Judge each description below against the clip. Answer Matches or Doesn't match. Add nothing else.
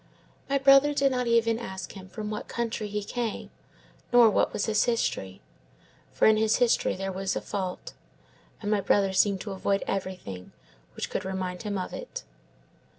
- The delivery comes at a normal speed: Matches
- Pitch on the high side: Matches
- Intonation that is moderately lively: Matches